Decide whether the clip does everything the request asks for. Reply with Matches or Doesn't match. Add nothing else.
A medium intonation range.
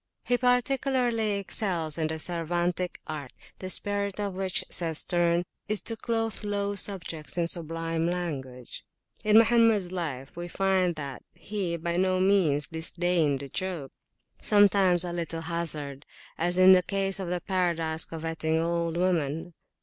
Matches